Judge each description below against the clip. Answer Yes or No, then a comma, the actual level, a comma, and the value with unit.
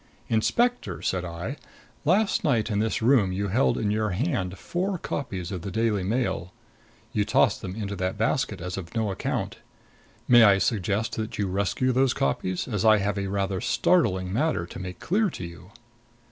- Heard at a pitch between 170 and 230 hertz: No, low, 105 Hz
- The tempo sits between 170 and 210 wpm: Yes, average, 180 wpm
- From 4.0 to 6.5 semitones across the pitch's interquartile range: Yes, average, 4.5 semitones